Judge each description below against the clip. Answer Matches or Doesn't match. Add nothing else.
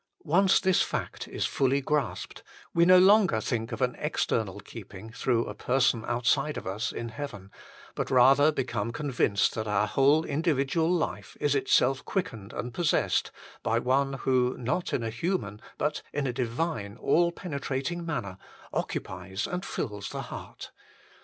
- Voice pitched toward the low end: Matches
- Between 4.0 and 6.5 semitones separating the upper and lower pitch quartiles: Matches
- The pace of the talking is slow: Doesn't match